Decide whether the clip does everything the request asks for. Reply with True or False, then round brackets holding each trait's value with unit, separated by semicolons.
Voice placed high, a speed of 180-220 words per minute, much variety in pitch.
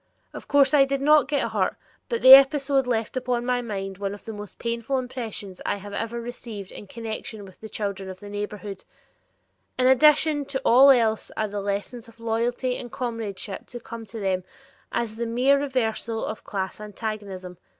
False (230 Hz; 185 wpm; 3.8 semitones)